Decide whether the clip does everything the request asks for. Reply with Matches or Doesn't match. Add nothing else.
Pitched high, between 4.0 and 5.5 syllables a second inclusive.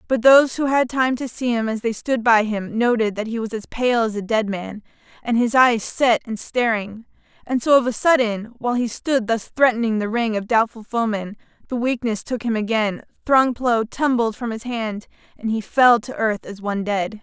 Matches